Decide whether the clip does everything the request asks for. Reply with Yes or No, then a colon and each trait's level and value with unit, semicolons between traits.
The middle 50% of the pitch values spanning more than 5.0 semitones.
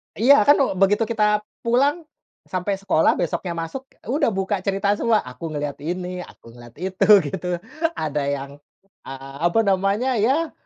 Yes: wide, 5.5 semitones